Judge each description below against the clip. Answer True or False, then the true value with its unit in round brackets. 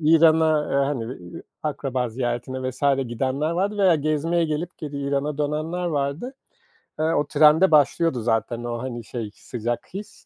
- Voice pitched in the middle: True (145 Hz)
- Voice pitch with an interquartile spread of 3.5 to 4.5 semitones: True (4.2 semitones)